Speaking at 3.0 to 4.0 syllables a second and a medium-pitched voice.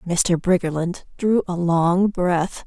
Yes: 3.5 syllables/s; medium, 175 Hz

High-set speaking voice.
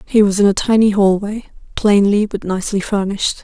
Yes: high, 205 Hz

